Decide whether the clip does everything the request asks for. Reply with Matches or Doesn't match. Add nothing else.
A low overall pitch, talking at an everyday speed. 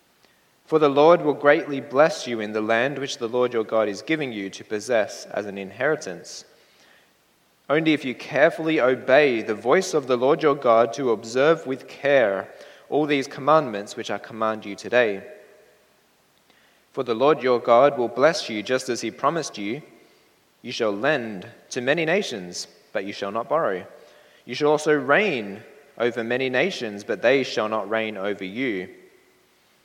Matches